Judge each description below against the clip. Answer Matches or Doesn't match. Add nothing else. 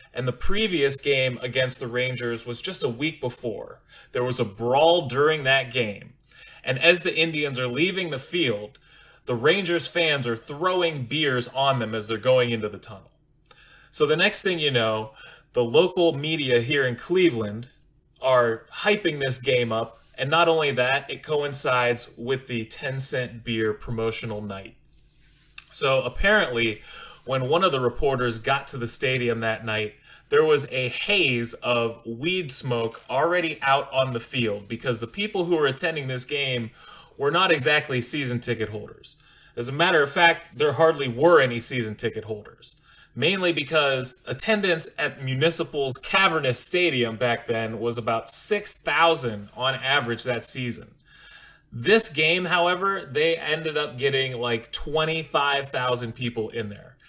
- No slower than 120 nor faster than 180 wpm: Matches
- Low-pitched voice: Matches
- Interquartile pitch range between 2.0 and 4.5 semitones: Doesn't match